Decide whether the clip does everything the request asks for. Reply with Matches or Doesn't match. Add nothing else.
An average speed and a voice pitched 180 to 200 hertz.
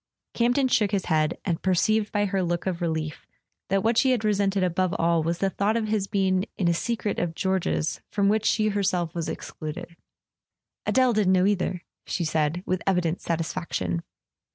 Matches